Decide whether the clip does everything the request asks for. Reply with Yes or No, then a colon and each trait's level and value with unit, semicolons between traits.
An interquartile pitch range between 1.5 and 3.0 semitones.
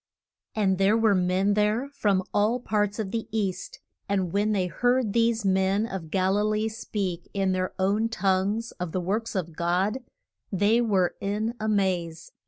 Yes: narrow, 2.6 semitones